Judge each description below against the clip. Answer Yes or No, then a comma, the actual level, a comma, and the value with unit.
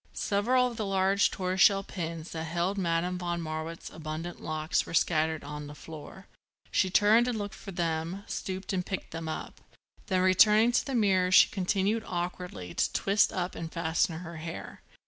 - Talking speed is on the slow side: No, average, 175 wpm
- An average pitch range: Yes, average, 3.2 semitones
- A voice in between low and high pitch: Yes, medium, 180 Hz